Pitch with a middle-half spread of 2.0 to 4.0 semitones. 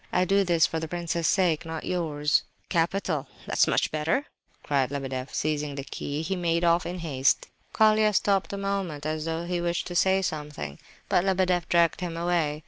Yes: average, 3.2 semitones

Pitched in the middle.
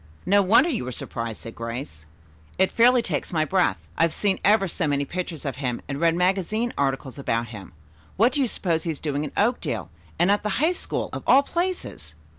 Yes: medium, 170 Hz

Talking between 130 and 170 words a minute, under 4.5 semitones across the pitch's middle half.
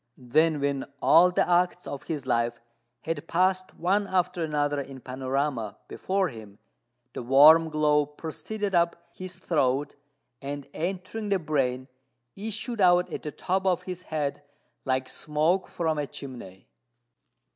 No: average, 140 wpm; average, 4.8 semitones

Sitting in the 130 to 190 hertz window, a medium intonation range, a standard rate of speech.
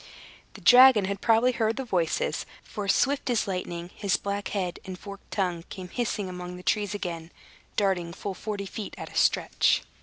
No: high, 200 Hz; average, 3.1 semitones; average, 180 wpm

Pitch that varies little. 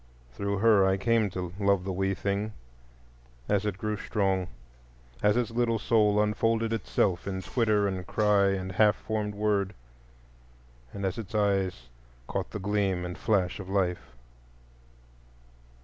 Yes: narrow, 2.0 semitones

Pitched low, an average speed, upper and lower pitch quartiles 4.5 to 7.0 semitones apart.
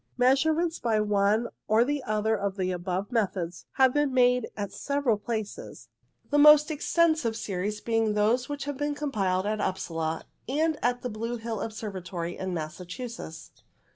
No: high, 220 Hz; average, 170 wpm; wide, 5.4 semitones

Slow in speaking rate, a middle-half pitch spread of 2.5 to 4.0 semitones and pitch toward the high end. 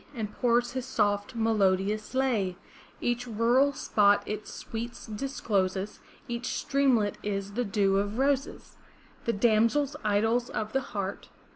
Yes: slow, 130 wpm; average, 3.2 semitones; high, 220 Hz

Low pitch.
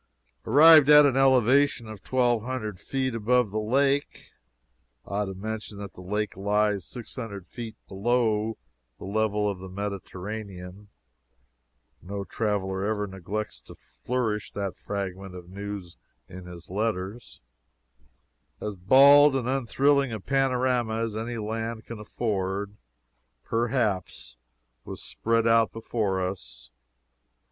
Yes: low, 110 Hz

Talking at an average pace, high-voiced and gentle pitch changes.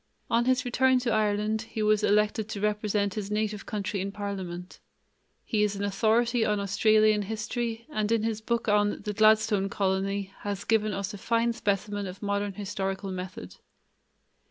Yes: average, 165 wpm; high, 210 Hz; narrow, 1.7 semitones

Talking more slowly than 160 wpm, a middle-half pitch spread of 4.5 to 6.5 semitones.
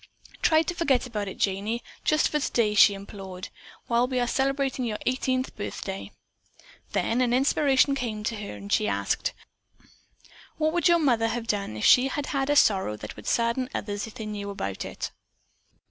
No: average, 180 wpm; average, 4.8 semitones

